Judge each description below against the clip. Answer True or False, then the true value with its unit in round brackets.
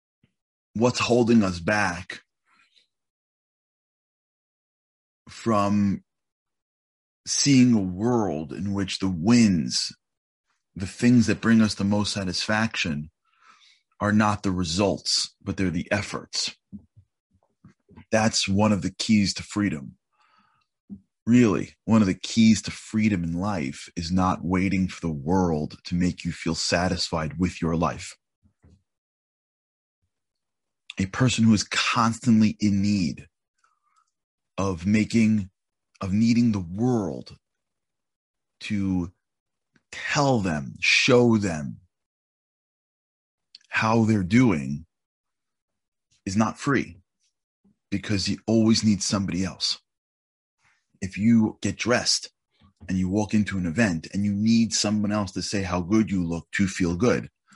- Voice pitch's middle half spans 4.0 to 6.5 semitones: False (3.5 semitones)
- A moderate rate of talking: False (115 wpm)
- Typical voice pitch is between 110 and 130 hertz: False (100 Hz)